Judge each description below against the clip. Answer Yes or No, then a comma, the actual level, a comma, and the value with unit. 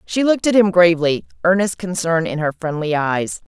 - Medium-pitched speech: Yes, medium, 175 Hz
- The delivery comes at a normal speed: Yes, average, 185 wpm